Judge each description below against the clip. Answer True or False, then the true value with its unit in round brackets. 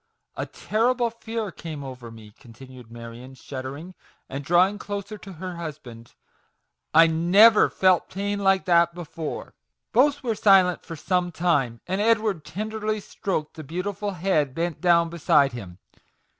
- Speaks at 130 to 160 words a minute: True (155 wpm)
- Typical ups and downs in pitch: False (6.1 semitones)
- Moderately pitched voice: True (175 Hz)